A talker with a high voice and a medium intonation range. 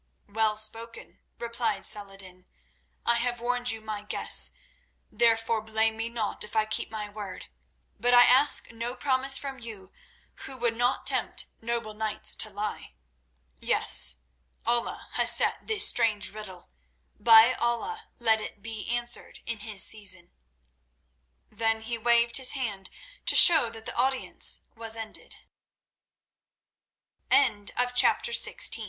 No: high, 225 Hz; narrow, 2.2 semitones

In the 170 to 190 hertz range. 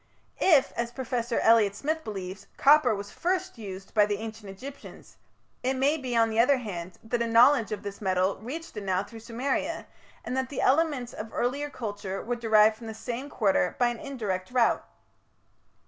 No: high, 230 Hz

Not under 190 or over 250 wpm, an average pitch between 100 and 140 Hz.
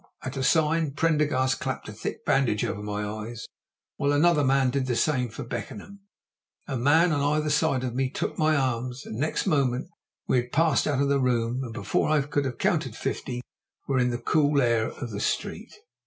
Yes: average, 200 wpm; low, 135 Hz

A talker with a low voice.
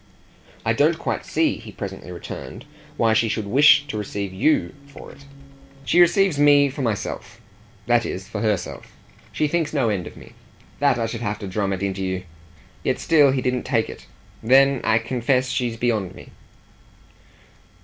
Yes: low, 120 Hz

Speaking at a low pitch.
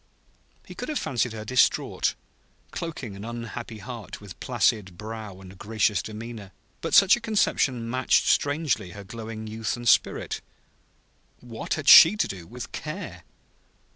Yes: low, 115 Hz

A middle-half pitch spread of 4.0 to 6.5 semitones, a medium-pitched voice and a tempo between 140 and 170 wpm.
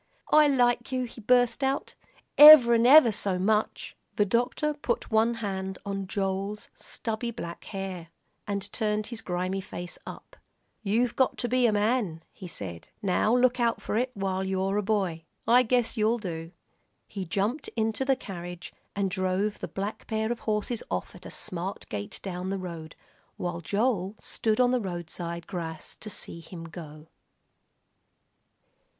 No: average, 4.4 semitones; high, 205 Hz; average, 160 wpm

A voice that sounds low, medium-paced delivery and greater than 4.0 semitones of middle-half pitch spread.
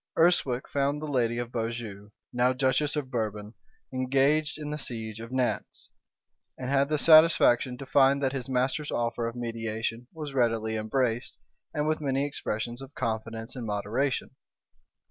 No: low, 125 Hz; average, 155 wpm; average, 3.4 semitones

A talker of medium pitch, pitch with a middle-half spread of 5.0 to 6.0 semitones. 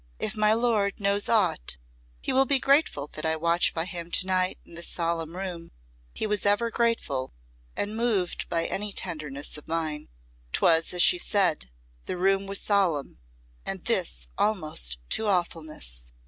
No: medium, 180 Hz; average, 4.5 semitones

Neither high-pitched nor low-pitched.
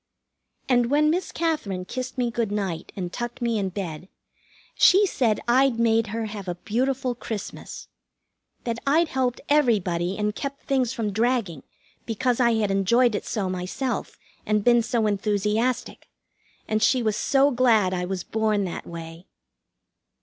No: high, 225 Hz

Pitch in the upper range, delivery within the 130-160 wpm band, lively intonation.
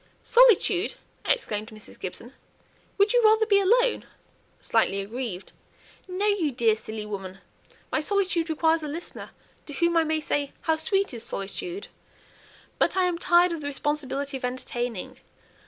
Yes: very high, 315 Hz; average, 150 wpm; wide, 7.8 semitones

